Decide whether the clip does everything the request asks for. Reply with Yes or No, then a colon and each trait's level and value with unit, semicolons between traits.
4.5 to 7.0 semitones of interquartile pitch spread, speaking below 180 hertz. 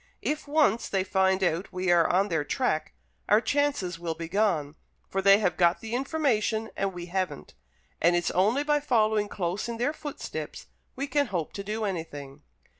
No: average, 5.1 semitones; high, 195 Hz